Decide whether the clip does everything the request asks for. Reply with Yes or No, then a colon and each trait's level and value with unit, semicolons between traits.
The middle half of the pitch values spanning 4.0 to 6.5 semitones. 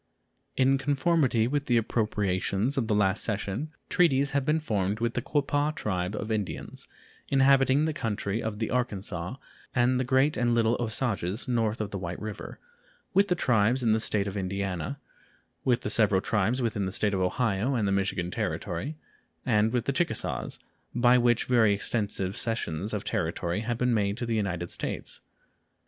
Yes: average, 4.4 semitones